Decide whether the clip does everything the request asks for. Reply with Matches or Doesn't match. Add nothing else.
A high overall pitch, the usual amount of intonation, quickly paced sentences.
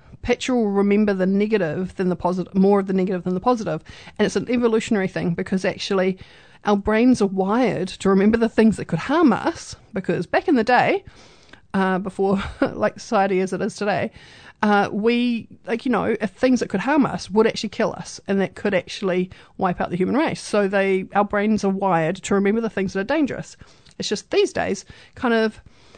Matches